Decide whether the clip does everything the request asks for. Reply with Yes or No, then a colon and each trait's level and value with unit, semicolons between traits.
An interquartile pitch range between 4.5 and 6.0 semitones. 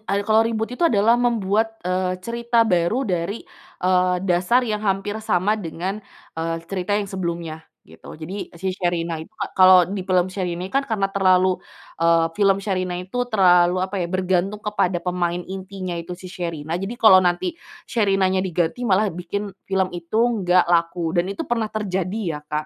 No: average, 2.7 semitones